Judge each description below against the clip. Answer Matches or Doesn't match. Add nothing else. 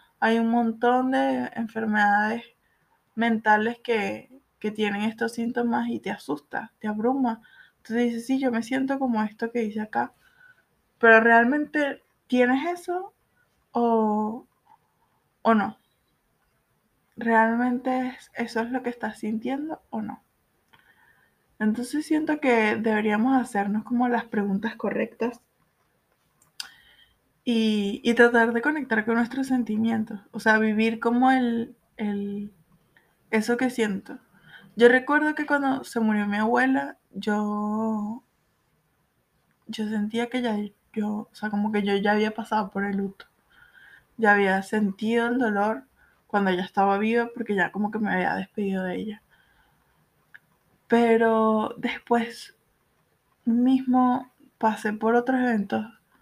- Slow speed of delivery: Matches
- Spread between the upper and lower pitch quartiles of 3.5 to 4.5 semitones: Doesn't match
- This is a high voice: Matches